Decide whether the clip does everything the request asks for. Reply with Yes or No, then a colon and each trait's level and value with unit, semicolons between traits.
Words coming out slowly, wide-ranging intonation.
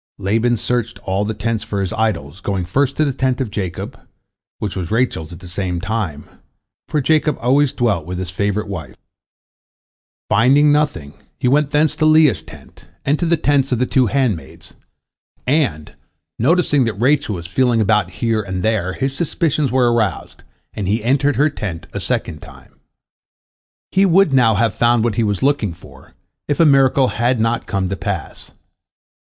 No: average, 180 wpm; wide, 5.9 semitones